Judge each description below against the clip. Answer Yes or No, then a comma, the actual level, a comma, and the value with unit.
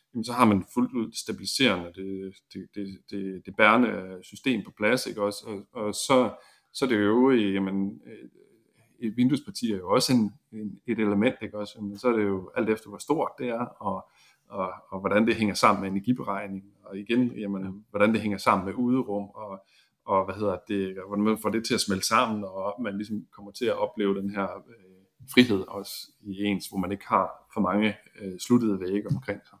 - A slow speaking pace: No, average, 215 wpm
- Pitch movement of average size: No, narrow, 2.3 semitones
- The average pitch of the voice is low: Yes, low, 100 Hz